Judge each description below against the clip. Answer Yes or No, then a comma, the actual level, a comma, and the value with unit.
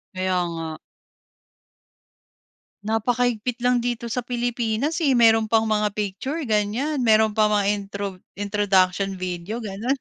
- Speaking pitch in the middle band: No, high, 220 Hz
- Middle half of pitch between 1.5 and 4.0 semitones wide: Yes, average, 3.3 semitones